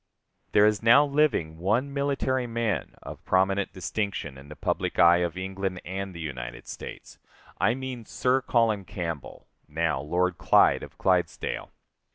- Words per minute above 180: No, average, 150 wpm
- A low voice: Yes, very low, 95 Hz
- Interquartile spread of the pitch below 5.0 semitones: No, wide, 5.6 semitones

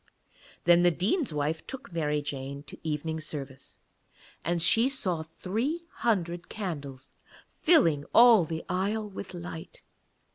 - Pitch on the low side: No, medium, 170 Hz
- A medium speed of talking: No, slow, 130 wpm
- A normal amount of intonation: No, wide, 5.7 semitones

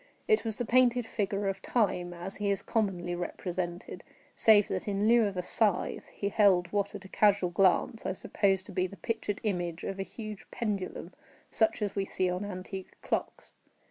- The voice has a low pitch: No, high, 195 Hz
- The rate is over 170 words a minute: Yes, average, 190 wpm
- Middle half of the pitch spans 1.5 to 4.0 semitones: Yes, narrow, 2.5 semitones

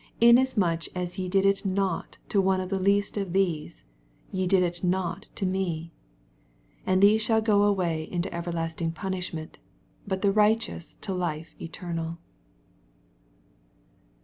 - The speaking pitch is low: No, medium, 185 Hz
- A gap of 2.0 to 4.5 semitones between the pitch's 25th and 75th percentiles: Yes, average, 2.7 semitones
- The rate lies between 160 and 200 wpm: No, average, 140 wpm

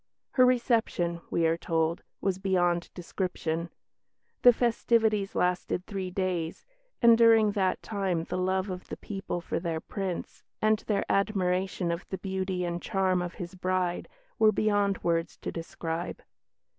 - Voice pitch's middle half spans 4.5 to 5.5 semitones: No, average, 2.7 semitones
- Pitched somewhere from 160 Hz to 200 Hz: Yes, medium, 185 Hz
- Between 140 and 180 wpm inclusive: Yes, average, 145 wpm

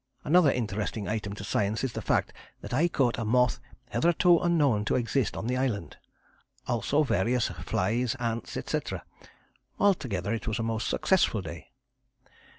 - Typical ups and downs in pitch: Yes, average, 4.3 semitones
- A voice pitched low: Yes, low, 115 Hz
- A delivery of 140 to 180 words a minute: Yes, average, 155 wpm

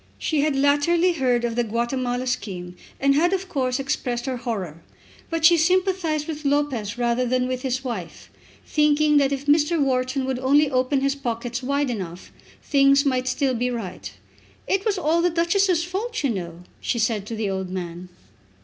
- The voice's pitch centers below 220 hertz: No, very high, 265 Hz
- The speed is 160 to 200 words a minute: Yes, average, 180 wpm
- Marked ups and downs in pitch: No, average, 4.1 semitones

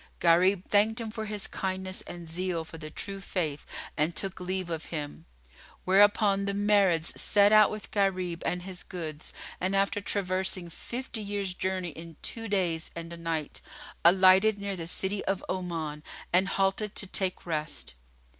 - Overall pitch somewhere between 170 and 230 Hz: Yes, medium, 185 Hz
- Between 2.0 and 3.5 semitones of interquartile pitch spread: Yes, average, 2.9 semitones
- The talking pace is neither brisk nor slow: Yes, average, 165 wpm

